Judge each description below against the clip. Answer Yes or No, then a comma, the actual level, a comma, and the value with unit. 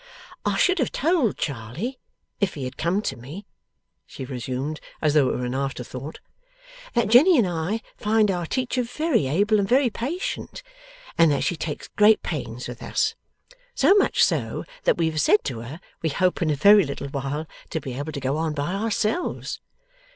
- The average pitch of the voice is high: No, medium, 170 Hz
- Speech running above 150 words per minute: Yes, average, 190 wpm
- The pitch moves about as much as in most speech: No, wide, 8.0 semitones